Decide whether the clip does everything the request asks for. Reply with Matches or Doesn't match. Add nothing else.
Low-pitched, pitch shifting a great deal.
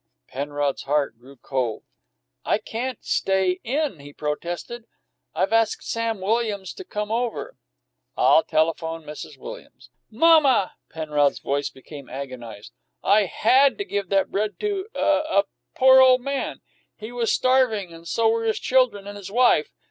Doesn't match